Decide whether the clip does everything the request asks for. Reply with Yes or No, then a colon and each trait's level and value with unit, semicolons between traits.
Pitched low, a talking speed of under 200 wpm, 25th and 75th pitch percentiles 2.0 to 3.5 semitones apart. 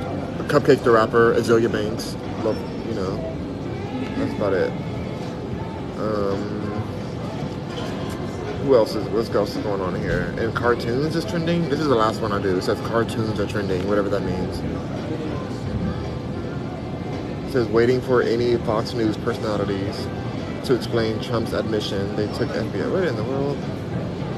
Yes: low, 110 Hz; average, 150 wpm; average, 2.7 semitones